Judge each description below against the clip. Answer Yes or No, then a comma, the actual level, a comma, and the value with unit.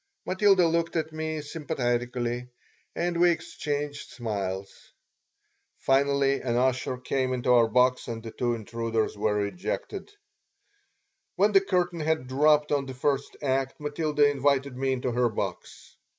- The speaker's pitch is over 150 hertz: No, low, 135 Hz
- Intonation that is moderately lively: Yes, average, 4.1 semitones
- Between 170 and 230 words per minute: No, slow, 135 wpm